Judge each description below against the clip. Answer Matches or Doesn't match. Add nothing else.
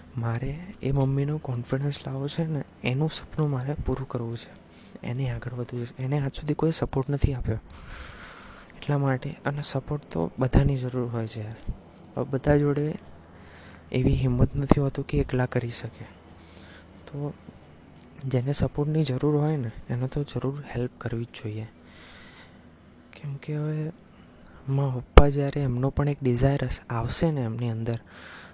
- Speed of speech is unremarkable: Doesn't match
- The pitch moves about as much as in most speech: Matches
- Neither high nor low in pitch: Doesn't match